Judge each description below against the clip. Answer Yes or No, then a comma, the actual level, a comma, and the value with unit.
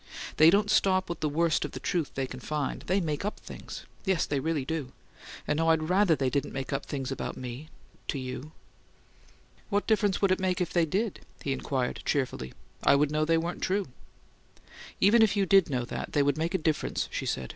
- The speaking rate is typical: No, fast, 210 wpm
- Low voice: No, medium, 160 Hz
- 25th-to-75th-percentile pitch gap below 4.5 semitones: No, average, 5.2 semitones